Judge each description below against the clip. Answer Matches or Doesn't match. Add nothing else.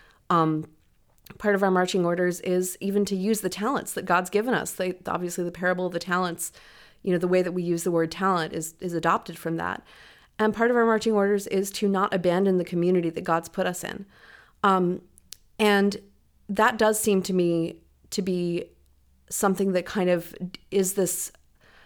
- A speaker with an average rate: Matches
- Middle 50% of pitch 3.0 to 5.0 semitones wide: Doesn't match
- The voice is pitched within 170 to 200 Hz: Matches